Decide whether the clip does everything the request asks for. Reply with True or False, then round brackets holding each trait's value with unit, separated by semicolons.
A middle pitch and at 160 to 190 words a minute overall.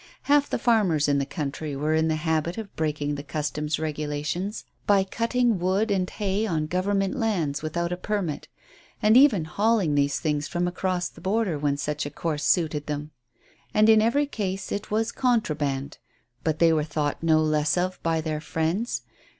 True (165 Hz; 180 wpm)